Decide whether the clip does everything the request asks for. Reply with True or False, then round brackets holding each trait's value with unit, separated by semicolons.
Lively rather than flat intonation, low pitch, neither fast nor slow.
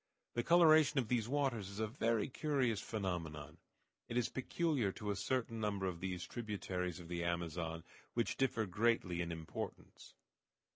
True (5.8 semitones; 105 Hz; 155 wpm)